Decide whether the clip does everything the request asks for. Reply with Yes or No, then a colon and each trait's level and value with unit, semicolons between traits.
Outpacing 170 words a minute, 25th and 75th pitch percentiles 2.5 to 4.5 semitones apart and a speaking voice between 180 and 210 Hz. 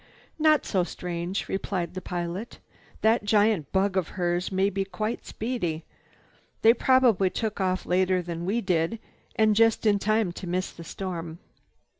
No: average, 155 wpm; average, 3.5 semitones; high, 190 Hz